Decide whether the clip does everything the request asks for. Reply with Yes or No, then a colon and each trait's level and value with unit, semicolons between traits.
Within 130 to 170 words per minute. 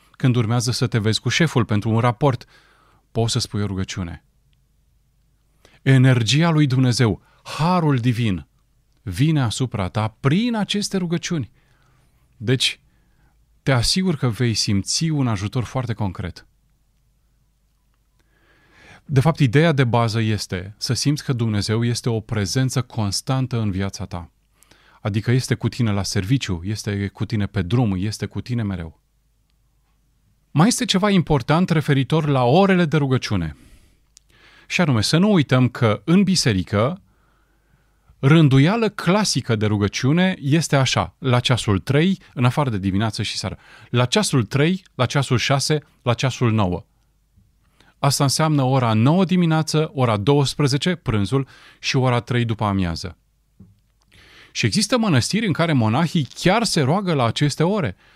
Yes: average, 140 wpm